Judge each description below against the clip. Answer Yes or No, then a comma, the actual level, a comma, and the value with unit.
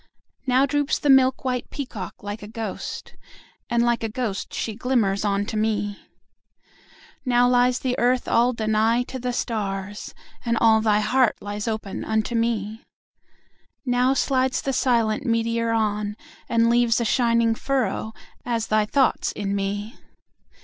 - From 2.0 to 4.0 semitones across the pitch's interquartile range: Yes, average, 2.7 semitones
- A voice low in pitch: No, high, 230 Hz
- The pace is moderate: Yes, average, 150 wpm